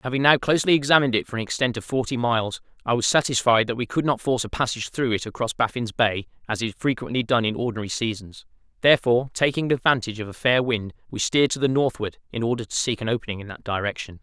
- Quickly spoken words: Yes, fast, 230 wpm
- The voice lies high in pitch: No, low, 120 Hz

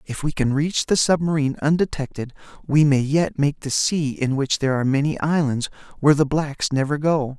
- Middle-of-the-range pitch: Yes, medium, 145 Hz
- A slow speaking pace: No, average, 195 wpm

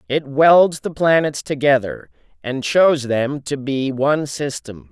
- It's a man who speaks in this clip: Yes, male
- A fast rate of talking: No, average, 145 wpm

